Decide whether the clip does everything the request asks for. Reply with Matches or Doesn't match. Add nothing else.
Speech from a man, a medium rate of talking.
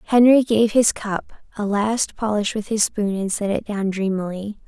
Doesn't match